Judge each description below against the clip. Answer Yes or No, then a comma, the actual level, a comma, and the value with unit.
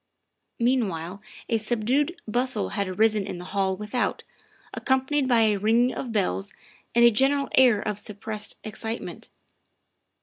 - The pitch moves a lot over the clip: No, average, 3.7 semitones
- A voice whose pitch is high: Yes, high, 220 Hz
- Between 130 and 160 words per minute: Yes, average, 140 wpm